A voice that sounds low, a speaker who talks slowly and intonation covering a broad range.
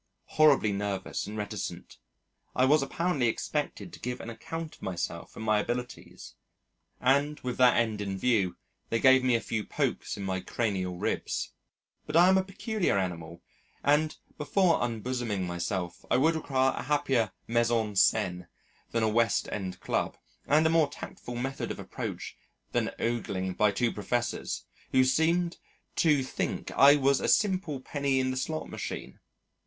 No: low, 125 Hz; average, 165 wpm; wide, 5.9 semitones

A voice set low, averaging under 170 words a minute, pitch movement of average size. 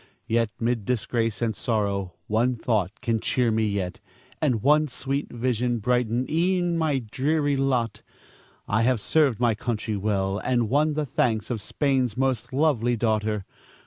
Yes: low, 120 Hz; average, 150 wpm; average, 3.6 semitones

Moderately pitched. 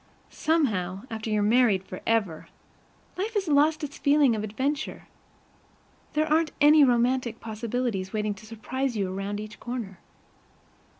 No: high, 235 Hz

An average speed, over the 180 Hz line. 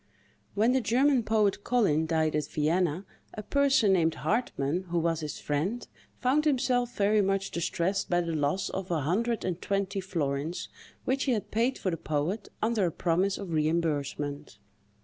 Yes: average, 170 wpm; high, 190 Hz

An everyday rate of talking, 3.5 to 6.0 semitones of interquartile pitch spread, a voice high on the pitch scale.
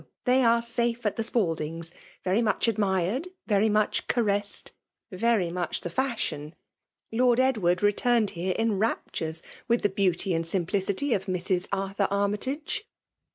Yes: average, 150 wpm; average, 4.3 semitones; high, 205 Hz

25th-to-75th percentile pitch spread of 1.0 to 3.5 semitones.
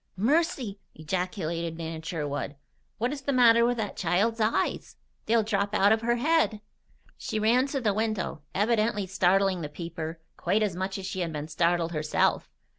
No: average, 5.2 semitones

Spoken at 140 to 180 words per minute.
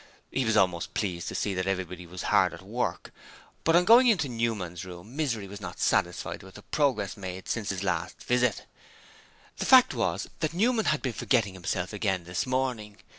No: average, 195 wpm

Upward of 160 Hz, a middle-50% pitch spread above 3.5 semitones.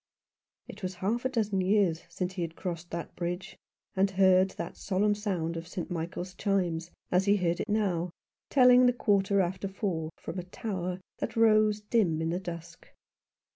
No: high, 190 Hz; average, 3.0 semitones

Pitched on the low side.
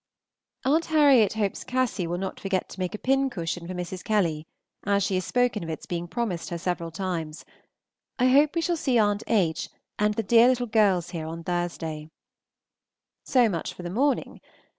No: high, 195 Hz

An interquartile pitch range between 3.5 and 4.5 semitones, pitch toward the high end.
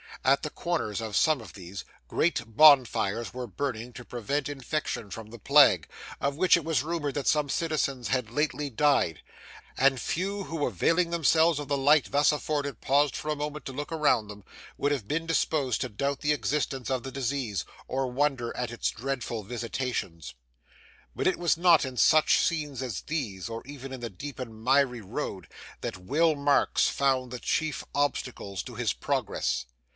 No: average, 4.1 semitones; low, 135 Hz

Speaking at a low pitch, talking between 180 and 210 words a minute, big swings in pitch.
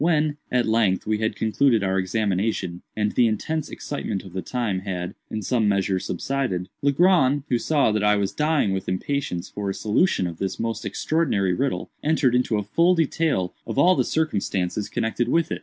Yes: low, 110 Hz; average, 190 wpm; wide, 6.5 semitones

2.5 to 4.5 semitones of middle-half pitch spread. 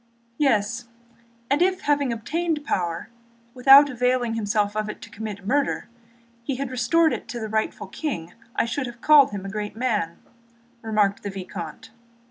No: average, 5.0 semitones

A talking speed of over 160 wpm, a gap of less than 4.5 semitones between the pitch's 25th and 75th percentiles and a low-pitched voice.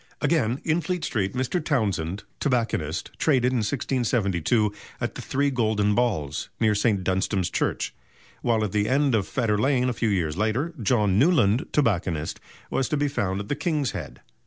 No: average, 170 wpm; average, 5.2 semitones; low, 115 Hz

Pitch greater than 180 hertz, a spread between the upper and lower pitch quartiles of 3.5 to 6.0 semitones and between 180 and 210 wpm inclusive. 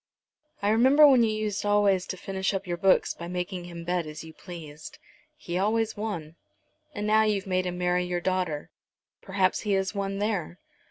No: high, 190 Hz; average, 2.7 semitones; average, 185 wpm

